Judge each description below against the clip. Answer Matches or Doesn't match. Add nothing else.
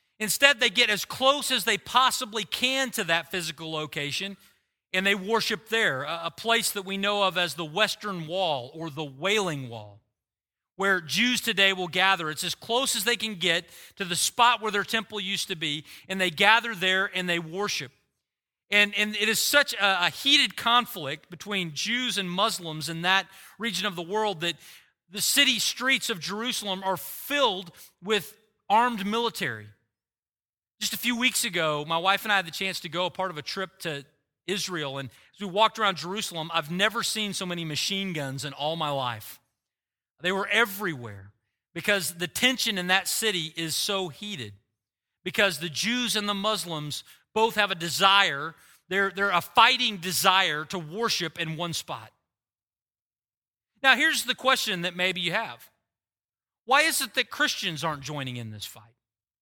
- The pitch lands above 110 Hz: Matches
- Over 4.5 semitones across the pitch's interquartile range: Matches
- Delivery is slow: Doesn't match